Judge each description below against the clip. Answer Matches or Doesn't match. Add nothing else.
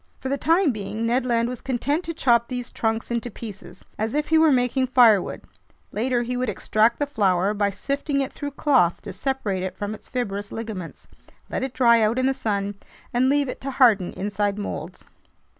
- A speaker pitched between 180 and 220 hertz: Doesn't match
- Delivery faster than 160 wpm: Matches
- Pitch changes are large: Doesn't match